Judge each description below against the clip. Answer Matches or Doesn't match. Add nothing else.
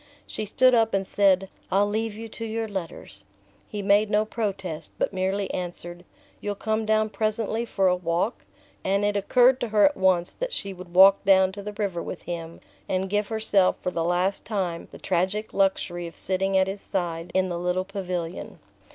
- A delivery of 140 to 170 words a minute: Doesn't match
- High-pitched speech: Matches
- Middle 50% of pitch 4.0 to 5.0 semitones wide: Doesn't match